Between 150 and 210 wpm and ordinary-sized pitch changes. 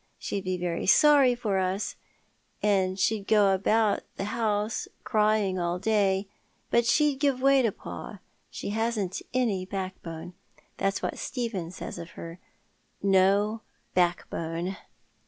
No: slow, 135 wpm; average, 3.2 semitones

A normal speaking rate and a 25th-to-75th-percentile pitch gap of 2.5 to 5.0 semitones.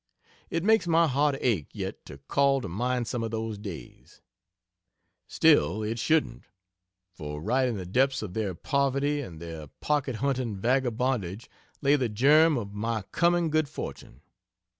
No: average, 155 wpm; wide, 5.4 semitones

